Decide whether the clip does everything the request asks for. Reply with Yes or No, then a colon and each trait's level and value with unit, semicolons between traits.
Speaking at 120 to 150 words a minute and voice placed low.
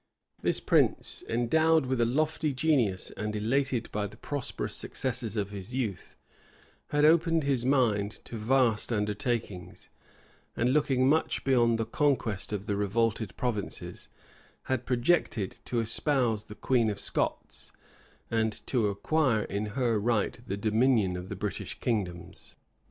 Yes: average, 140 wpm; low, 115 Hz